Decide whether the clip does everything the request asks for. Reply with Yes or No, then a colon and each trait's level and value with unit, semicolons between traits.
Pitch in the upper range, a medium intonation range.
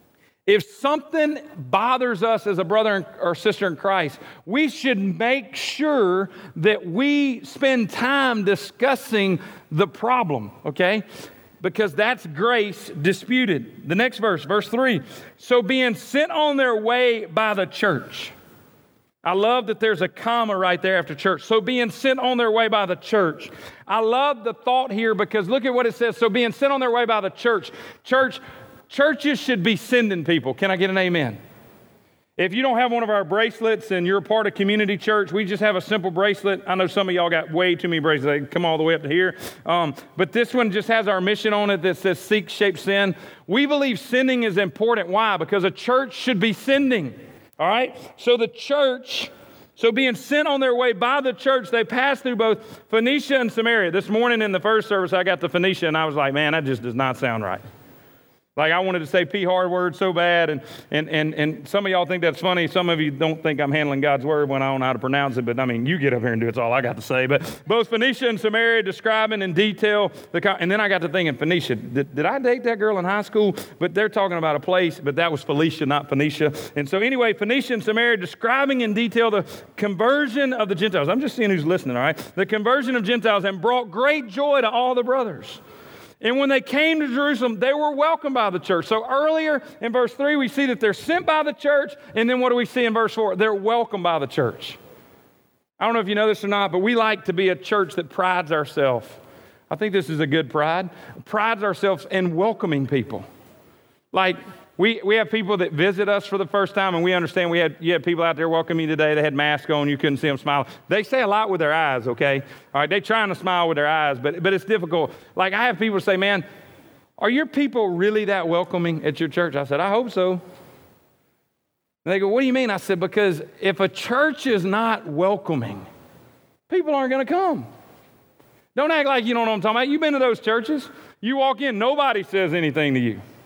No: high, 205 Hz; wide, 5.7 semitones